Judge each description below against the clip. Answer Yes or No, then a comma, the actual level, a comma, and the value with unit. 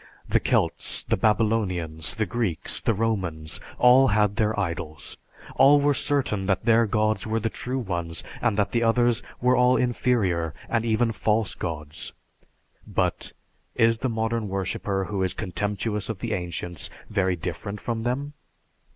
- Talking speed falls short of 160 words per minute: Yes, average, 150 wpm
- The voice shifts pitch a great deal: No, average, 4.0 semitones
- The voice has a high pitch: No, low, 110 Hz